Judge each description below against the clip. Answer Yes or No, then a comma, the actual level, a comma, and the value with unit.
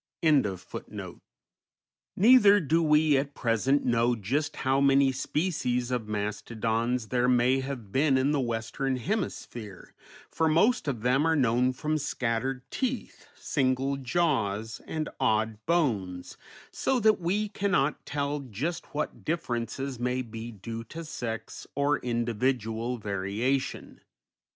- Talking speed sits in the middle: No, slow, 125 wpm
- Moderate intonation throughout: Yes, average, 4.6 semitones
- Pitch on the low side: Yes, low, 130 Hz